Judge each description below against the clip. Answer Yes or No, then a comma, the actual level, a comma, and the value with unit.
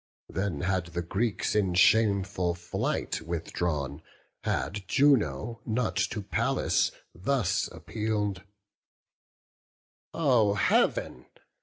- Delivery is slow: Yes, slow, 90 wpm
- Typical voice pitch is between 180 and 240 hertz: No, very low, 95 Hz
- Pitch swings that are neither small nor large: Yes, average, 4.1 semitones